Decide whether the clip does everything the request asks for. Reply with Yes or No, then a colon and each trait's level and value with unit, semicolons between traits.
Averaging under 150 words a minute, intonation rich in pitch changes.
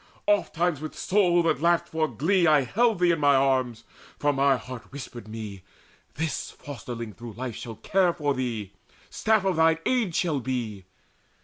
No: average, 170 wpm; wide, 6.0 semitones